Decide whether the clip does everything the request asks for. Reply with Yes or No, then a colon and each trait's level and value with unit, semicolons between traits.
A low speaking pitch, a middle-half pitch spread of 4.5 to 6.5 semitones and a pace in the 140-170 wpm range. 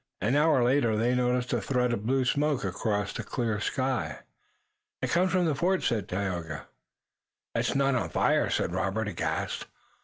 Yes: low, 125 Hz; average, 4.9 semitones; average, 165 wpm